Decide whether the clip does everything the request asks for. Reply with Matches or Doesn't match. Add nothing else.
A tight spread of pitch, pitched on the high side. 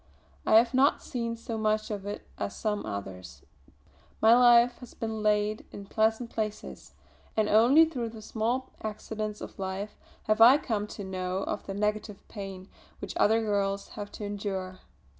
Matches